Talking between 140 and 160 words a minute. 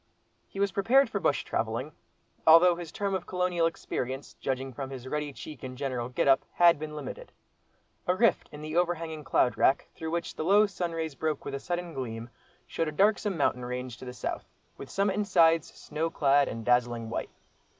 No: average, 195 wpm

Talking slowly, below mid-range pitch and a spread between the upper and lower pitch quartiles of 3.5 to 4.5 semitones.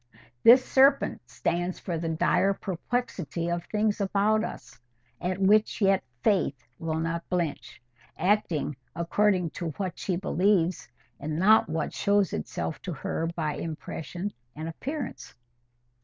No: slow, 130 wpm; medium, 180 Hz; average, 4.0 semitones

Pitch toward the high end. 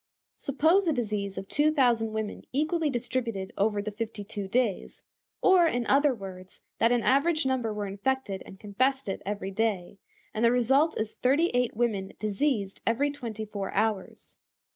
Yes: high, 230 Hz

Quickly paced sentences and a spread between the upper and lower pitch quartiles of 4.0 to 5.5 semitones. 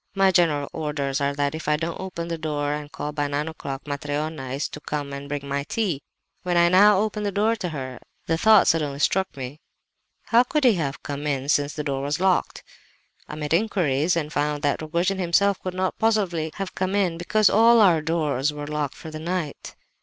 Yes: fast, 210 wpm; average, 4.3 semitones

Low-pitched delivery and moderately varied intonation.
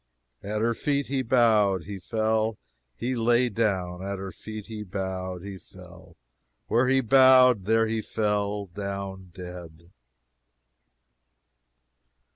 Yes: low, 105 Hz; average, 3.4 semitones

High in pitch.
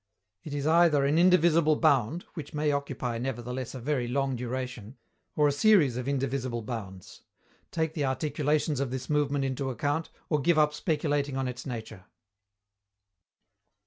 No: medium, 140 Hz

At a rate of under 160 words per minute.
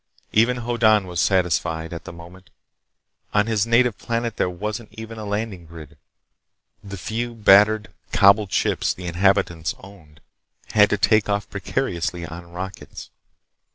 Yes: average, 145 wpm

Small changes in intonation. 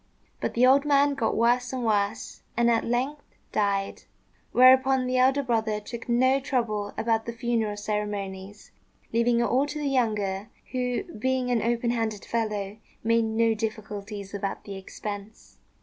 No: average, 3.3 semitones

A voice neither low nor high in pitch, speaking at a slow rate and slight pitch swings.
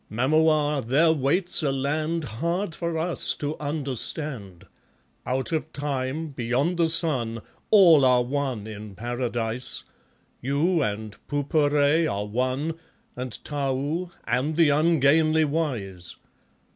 No: medium, 145 Hz; slow, 115 wpm; average, 4.1 semitones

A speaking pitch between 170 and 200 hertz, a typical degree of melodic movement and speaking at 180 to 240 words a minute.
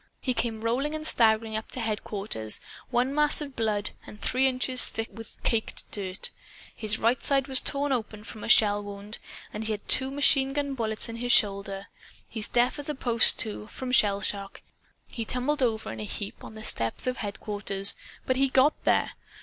No: high, 225 Hz; average, 3.8 semitones; average, 195 wpm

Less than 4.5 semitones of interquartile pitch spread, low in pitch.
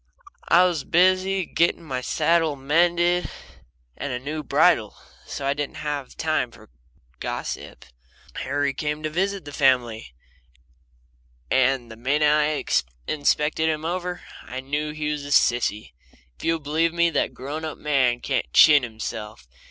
No: average, 3.6 semitones; medium, 150 Hz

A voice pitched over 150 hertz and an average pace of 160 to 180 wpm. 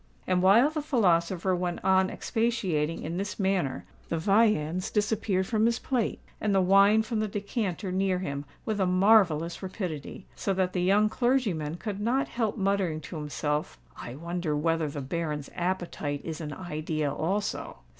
Yes: medium, 185 Hz; average, 165 wpm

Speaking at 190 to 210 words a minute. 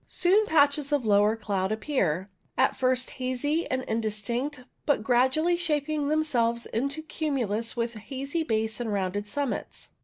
No: average, 140 wpm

